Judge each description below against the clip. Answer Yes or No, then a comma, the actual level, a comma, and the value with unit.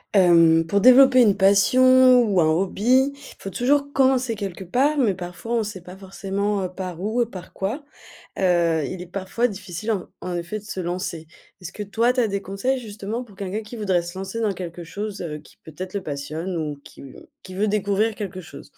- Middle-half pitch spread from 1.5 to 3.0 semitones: No, average, 4.0 semitones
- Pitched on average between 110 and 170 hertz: No, high, 195 Hz